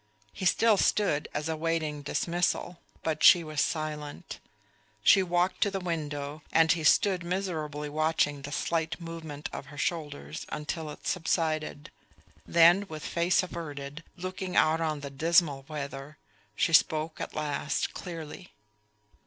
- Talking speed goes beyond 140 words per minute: No, slow, 135 wpm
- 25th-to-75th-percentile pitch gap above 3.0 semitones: No, narrow, 2.5 semitones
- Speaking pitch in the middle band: Yes, medium, 160 Hz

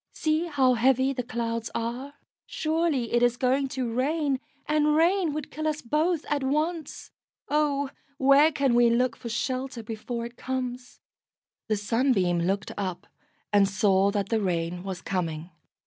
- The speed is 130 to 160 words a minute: Yes, average, 155 wpm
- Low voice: No, very high, 255 Hz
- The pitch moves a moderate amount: Yes, average, 4.7 semitones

